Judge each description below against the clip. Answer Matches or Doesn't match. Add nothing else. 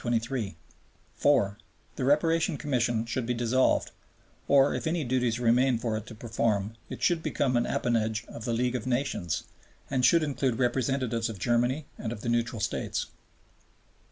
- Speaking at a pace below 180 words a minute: Matches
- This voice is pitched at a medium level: Doesn't match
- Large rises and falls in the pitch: Doesn't match